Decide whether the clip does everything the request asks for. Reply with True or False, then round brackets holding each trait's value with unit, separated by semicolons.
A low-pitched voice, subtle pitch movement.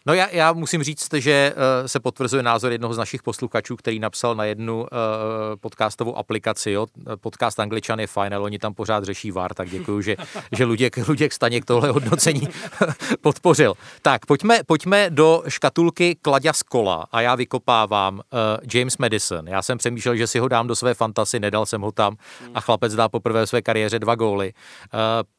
False (115 Hz; 4.2 semitones)